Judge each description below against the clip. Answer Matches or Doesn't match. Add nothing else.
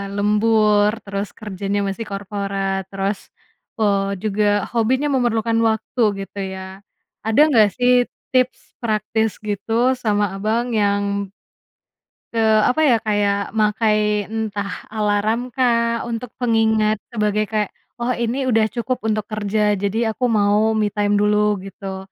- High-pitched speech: Matches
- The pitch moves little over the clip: Matches